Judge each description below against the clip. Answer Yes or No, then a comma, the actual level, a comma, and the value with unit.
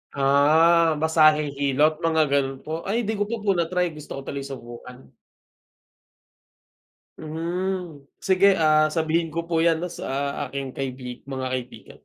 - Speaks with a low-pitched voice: No, medium, 155 Hz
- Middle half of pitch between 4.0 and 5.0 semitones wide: No, average, 3.4 semitones